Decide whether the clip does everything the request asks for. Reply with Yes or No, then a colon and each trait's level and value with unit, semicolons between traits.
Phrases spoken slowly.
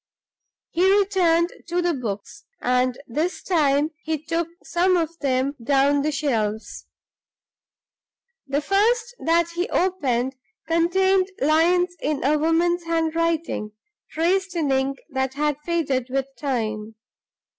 Yes: slow, 125 wpm